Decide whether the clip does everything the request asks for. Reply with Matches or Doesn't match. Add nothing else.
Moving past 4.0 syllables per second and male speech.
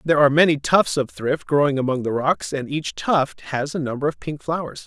Matches